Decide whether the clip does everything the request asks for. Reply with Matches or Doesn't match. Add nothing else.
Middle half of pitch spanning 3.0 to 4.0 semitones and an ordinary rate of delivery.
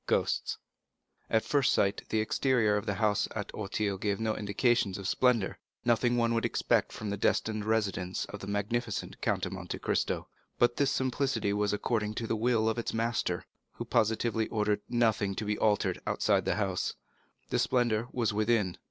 Doesn't match